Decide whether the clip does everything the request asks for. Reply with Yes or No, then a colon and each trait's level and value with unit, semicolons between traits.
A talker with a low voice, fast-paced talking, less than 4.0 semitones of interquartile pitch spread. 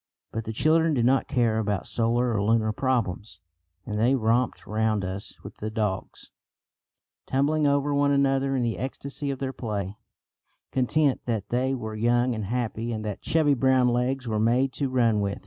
No: low, 120 Hz; average, 180 wpm; average, 3.6 semitones